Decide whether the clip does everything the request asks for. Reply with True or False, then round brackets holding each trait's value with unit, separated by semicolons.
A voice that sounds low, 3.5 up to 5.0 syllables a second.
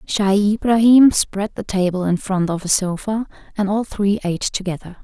False (200 Hz; 4.9 syllables/s)